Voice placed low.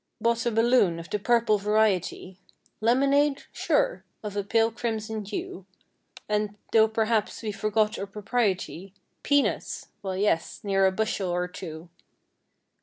No: high, 210 Hz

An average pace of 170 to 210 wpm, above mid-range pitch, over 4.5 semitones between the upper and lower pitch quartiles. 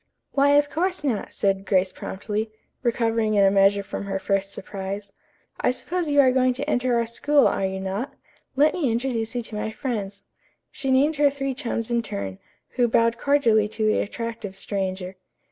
Yes: average, 185 wpm; high, 230 Hz; average, 5.0 semitones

